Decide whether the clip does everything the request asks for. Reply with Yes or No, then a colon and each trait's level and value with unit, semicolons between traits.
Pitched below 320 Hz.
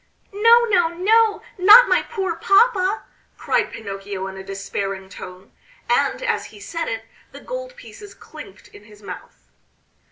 No: very high, 335 Hz